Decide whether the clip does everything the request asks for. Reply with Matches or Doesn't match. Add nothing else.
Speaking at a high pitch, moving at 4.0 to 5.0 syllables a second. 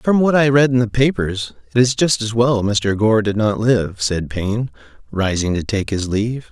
Doesn't match